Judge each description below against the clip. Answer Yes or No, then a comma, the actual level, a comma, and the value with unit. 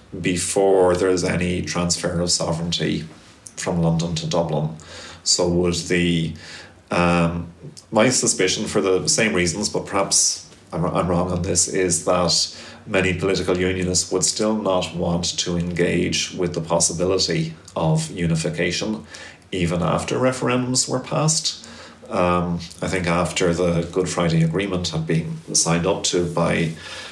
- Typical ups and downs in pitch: No, narrow, 1.7 semitones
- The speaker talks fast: No, average, 140 wpm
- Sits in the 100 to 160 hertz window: No, very low, 85 Hz